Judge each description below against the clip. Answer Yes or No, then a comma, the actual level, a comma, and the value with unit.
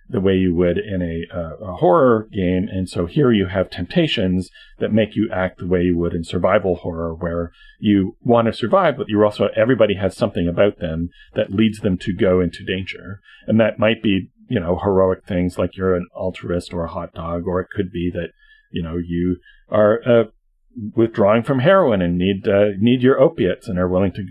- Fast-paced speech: Yes, fast, 210 wpm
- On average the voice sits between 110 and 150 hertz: No, very low, 95 Hz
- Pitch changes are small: No, average, 3.3 semitones